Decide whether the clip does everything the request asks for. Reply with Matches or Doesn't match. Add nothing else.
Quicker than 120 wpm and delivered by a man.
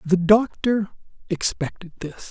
Doesn't match